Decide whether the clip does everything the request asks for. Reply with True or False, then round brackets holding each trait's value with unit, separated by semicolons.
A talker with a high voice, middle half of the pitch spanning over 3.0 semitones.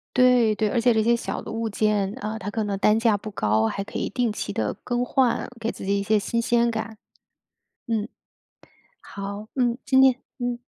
False (220 Hz; 2.5 semitones)